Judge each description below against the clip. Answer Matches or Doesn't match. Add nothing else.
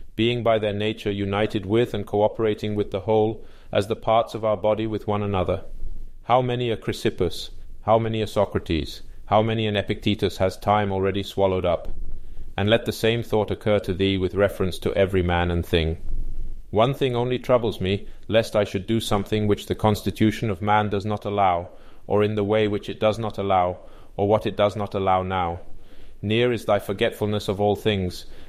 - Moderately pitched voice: Doesn't match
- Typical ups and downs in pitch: Doesn't match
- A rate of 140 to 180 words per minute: Doesn't match